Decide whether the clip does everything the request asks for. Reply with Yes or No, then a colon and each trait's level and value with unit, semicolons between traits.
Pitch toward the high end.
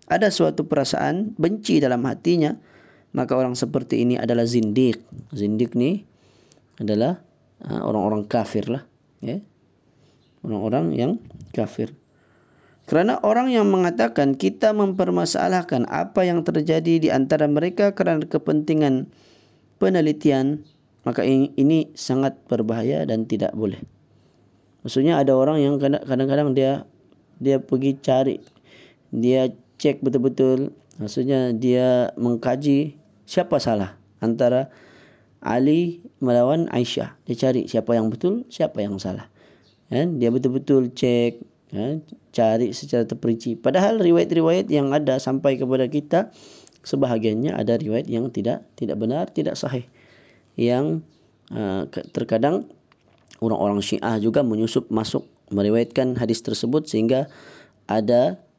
No: low, 130 Hz